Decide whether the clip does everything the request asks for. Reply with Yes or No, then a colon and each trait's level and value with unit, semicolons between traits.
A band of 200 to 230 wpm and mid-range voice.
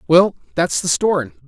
Yes: fast, 205 wpm; medium, 175 Hz